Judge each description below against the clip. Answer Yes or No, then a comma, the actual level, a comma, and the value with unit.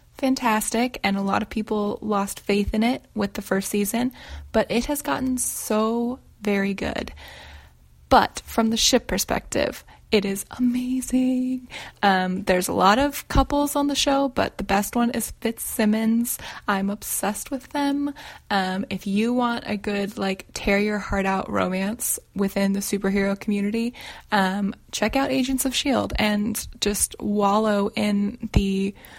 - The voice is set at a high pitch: Yes, high, 210 Hz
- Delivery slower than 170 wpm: Yes, average, 155 wpm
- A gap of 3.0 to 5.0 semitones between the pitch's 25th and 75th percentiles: Yes, average, 3.7 semitones